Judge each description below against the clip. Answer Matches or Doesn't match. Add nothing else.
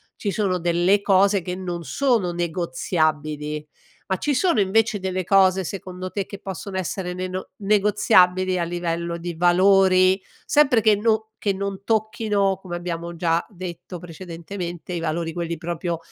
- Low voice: Doesn't match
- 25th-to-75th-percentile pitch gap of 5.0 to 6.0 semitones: Doesn't match